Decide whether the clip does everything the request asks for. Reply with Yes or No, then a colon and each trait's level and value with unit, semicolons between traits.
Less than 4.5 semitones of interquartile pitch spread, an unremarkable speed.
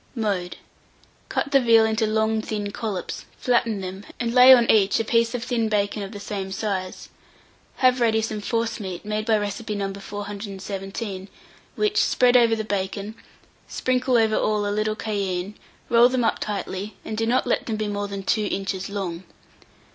Yes: narrow, 2.5 semitones; average, 175 wpm